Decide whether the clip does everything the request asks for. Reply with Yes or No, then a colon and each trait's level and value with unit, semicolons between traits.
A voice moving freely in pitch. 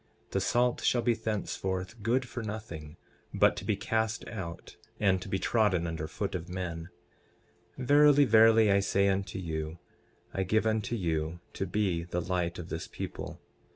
No: average, 4.3 semitones